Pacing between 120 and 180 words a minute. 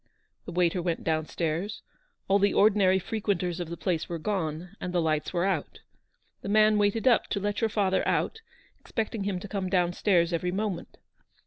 No: average, 190 wpm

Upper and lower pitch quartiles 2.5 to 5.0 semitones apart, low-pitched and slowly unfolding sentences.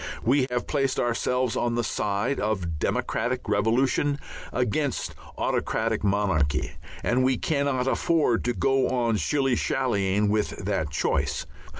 Yes: average, 4.2 semitones; low, 120 Hz; slow, 125 wpm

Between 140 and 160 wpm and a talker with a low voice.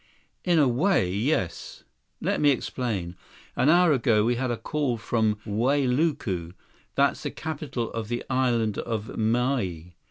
Yes: average, 145 wpm; low, 120 Hz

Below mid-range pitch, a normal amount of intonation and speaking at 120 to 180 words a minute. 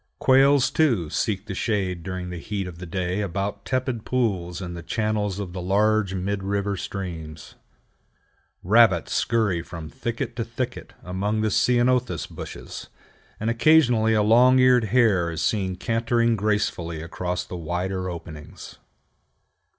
Yes: low, 100 Hz; average, 4.4 semitones; average, 145 wpm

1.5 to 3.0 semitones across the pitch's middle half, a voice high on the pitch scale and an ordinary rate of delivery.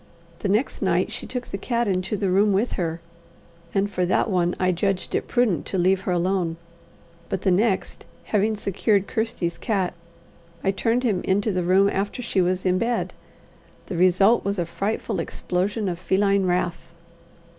Yes: narrow, 2.4 semitones; high, 195 Hz; average, 175 wpm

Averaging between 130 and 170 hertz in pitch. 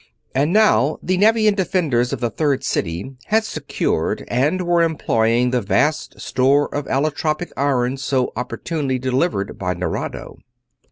Yes: low, 135 Hz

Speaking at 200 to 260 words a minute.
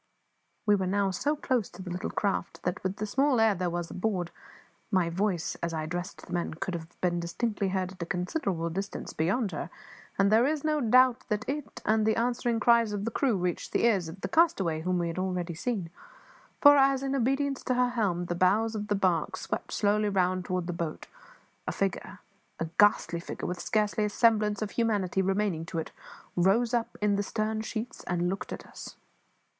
Yes: fast, 205 wpm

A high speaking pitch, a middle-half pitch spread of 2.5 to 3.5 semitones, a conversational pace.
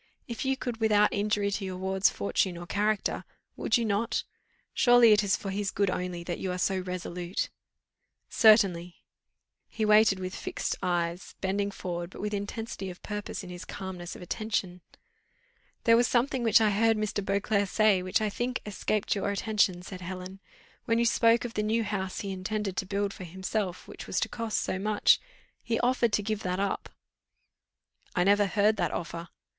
Yes: high, 200 Hz; average, 2.8 semitones; average, 185 wpm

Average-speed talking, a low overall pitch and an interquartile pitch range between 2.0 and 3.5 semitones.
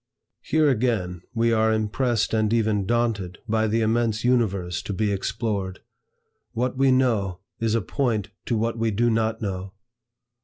Yes: average, 155 wpm; low, 110 Hz; average, 2.7 semitones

